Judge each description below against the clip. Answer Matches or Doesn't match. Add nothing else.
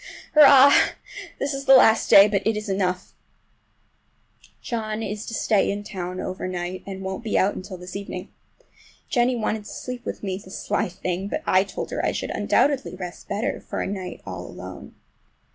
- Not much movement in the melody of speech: Doesn't match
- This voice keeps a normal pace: Matches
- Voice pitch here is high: Matches